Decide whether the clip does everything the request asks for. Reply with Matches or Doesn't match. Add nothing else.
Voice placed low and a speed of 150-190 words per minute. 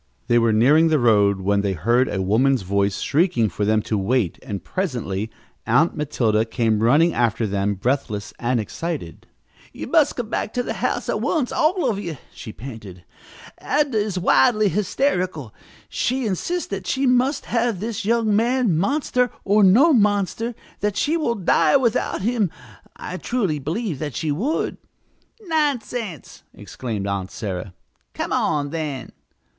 Doesn't match